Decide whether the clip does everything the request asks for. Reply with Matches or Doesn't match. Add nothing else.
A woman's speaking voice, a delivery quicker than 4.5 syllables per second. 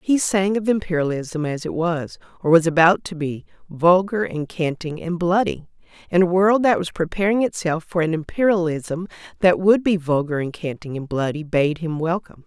Matches